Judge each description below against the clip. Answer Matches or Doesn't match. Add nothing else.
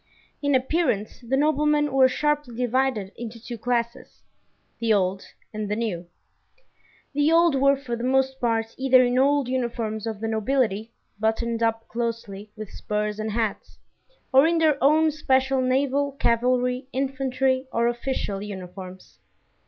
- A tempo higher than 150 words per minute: Doesn't match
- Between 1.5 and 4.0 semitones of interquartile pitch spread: Matches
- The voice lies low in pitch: Doesn't match